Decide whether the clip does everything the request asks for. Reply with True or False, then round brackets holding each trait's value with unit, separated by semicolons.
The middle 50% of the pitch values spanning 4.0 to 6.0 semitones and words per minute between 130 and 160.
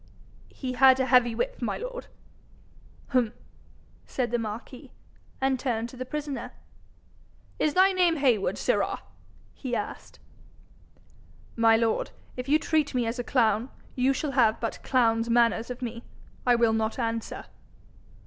False (2.9 semitones; 145 wpm)